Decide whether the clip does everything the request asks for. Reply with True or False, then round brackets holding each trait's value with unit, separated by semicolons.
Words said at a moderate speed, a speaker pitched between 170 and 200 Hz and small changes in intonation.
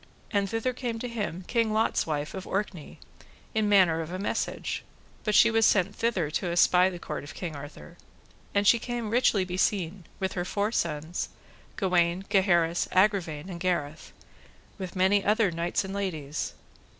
False (165 wpm; 190 Hz; 3.5 semitones)